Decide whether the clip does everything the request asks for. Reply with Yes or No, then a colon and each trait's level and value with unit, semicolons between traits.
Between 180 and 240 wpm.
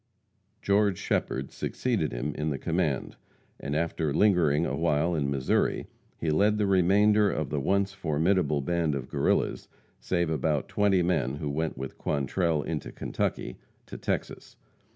No: average, 145 wpm